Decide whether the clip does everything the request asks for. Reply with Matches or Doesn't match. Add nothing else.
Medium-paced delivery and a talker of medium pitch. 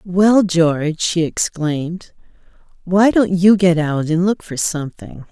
Matches